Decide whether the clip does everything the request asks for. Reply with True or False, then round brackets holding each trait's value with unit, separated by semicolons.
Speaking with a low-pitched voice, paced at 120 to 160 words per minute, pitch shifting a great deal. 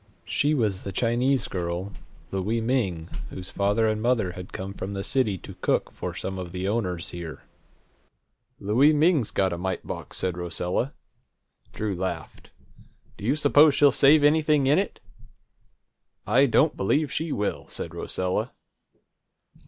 True (105 Hz; 150 wpm; 6.7 semitones)